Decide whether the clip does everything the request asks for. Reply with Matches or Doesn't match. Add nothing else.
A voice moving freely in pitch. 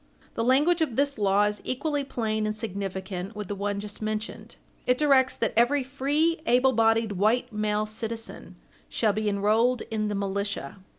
Doesn't match